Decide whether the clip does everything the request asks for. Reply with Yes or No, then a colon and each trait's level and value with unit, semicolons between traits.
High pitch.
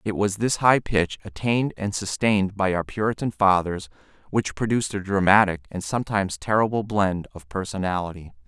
No: low, 100 Hz